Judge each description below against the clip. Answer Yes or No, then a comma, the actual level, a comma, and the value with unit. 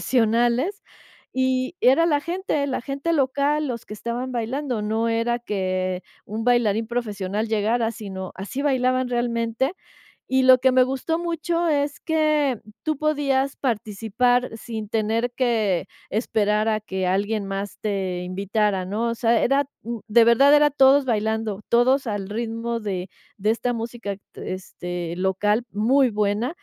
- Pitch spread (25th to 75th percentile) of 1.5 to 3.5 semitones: No, average, 3.9 semitones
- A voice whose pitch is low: No, high, 235 Hz